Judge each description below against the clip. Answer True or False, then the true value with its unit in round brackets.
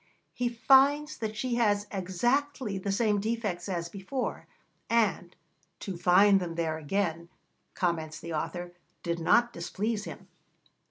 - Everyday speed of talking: False (130 wpm)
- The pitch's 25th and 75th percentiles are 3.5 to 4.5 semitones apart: False (5.1 semitones)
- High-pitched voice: True (200 Hz)